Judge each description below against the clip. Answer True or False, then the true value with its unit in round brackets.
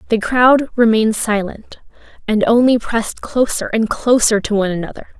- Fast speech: False (150 wpm)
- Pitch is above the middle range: True (225 Hz)